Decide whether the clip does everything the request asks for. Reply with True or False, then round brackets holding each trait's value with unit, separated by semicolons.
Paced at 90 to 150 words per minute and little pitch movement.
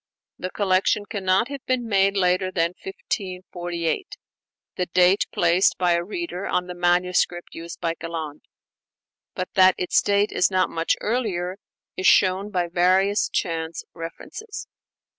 True (140 wpm; 2.3 semitones)